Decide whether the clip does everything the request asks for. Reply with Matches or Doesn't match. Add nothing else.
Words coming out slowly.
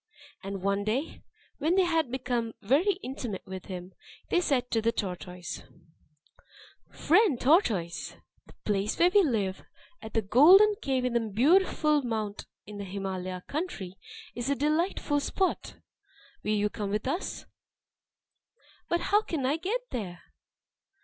Doesn't match